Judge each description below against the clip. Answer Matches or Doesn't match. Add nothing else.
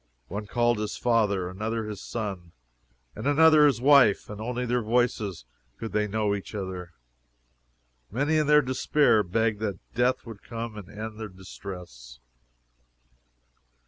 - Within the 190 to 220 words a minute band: Doesn't match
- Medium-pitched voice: Doesn't match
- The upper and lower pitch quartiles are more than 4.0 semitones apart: Doesn't match